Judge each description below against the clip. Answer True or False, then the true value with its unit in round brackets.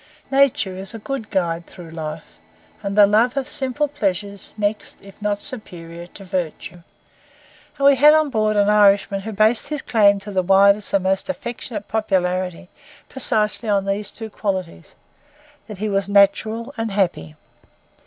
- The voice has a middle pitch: False (205 Hz)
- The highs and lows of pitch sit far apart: False (2.8 semitones)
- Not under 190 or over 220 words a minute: False (160 wpm)